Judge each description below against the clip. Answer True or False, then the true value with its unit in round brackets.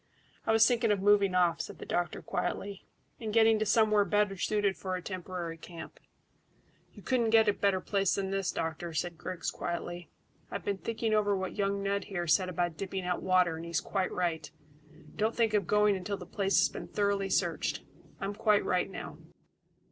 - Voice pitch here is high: True (195 Hz)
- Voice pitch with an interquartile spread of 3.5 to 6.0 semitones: False (2.7 semitones)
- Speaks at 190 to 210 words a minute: True (195 wpm)